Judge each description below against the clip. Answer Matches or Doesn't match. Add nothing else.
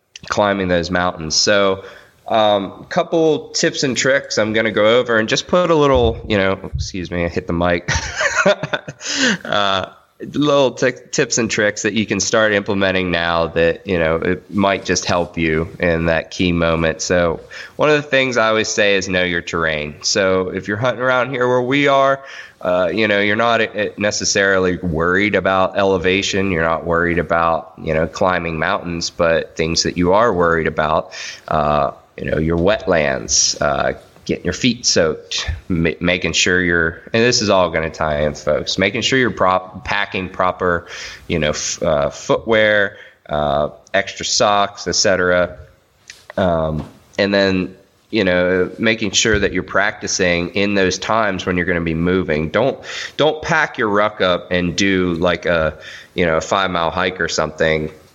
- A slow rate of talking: Doesn't match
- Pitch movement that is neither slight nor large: Matches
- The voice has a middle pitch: Doesn't match